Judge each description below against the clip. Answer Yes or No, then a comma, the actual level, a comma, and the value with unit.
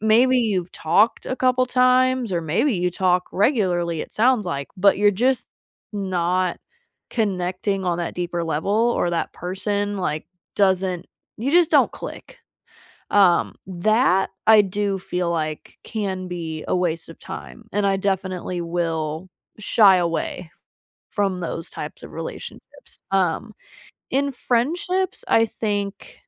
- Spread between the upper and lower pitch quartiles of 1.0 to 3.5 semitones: No, average, 4.0 semitones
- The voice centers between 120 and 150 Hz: No, high, 195 Hz